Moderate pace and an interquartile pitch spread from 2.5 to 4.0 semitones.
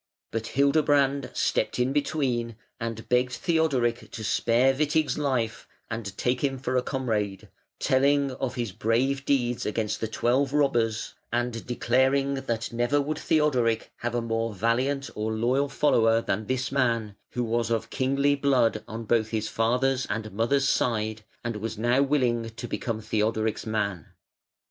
Yes: average, 155 wpm; average, 3.2 semitones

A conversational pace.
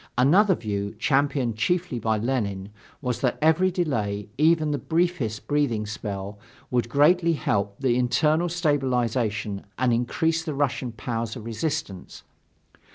No: slow, 130 wpm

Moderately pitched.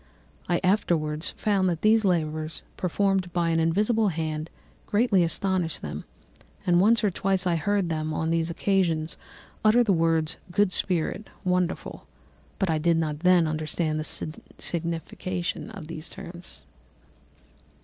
Yes: medium, 175 Hz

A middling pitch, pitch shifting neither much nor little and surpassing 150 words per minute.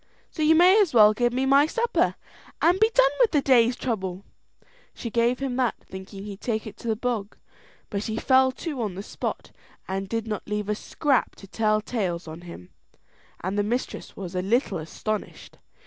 No: high, 225 Hz; average, 4.7 semitones; average, 195 wpm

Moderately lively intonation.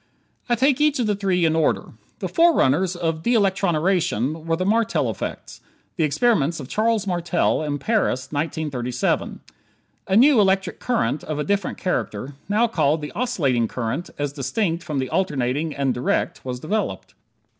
No: wide, 6.4 semitones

